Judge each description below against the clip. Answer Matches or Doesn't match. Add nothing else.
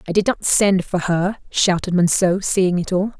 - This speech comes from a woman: Matches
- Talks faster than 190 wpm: Matches